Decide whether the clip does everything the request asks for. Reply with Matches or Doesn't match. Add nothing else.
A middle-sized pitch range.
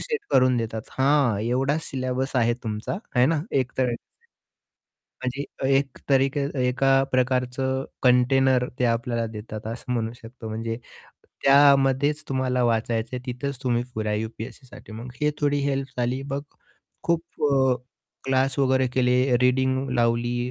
Doesn't match